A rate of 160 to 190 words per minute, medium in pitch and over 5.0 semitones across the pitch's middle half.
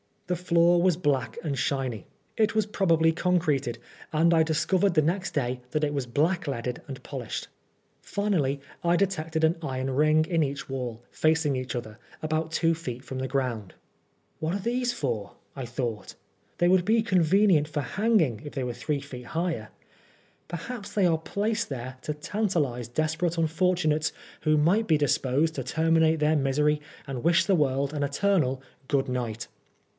No: average, 170 wpm; medium, 155 Hz; average, 4.6 semitones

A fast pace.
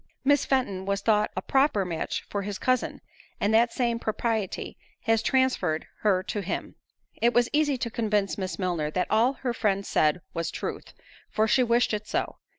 No: average, 180 wpm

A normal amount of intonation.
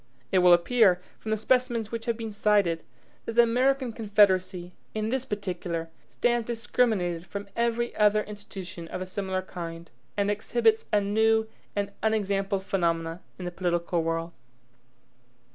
Yes: average, 3.9 semitones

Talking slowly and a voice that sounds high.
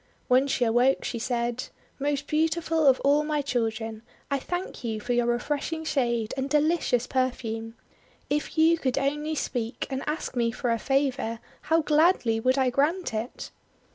No: average, 170 wpm; very high, 265 Hz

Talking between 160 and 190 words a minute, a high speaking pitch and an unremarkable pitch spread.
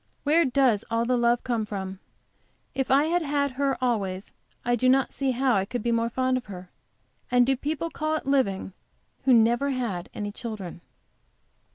Yes: average, 185 wpm; high, 245 Hz; average, 4.0 semitones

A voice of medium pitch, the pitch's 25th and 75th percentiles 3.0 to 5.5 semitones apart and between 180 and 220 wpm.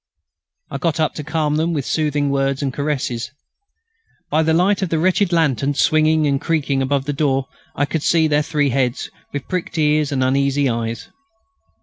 No: medium, 145 Hz; narrow, 2.5 semitones; average, 185 wpm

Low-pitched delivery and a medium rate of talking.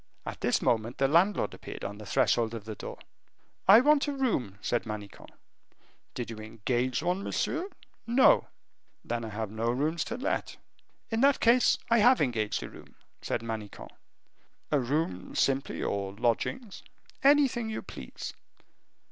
Yes: low, 130 Hz; average, 155 wpm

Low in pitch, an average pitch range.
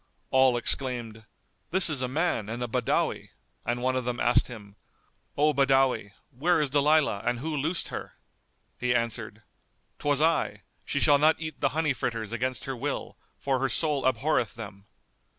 Yes: low, 130 Hz; average, 3.8 semitones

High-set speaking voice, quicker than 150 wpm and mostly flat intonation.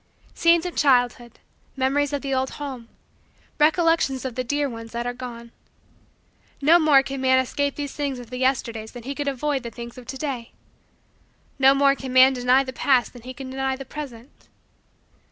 Yes: very high, 265 Hz; average, 190 wpm; narrow, 2.3 semitones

